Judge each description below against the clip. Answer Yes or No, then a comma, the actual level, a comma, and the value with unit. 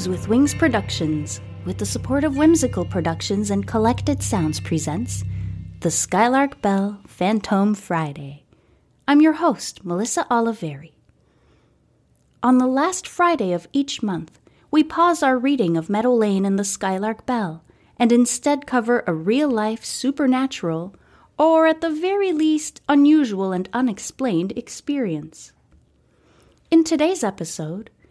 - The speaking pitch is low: No, high, 220 Hz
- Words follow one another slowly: Yes, slow, 130 wpm